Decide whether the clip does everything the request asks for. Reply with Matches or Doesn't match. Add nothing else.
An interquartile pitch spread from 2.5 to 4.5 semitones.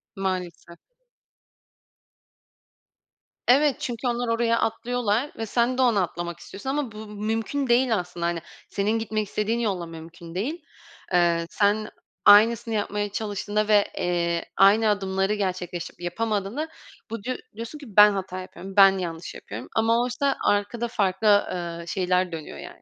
Matches